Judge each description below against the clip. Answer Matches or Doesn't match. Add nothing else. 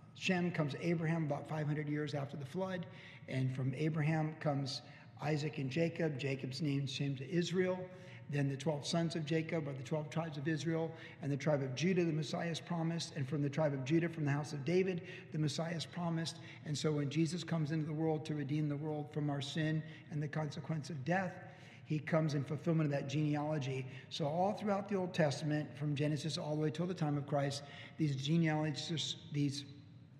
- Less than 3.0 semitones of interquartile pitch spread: Matches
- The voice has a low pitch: Doesn't match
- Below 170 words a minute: Doesn't match